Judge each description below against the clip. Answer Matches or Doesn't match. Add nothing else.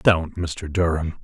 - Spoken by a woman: Doesn't match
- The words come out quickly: Doesn't match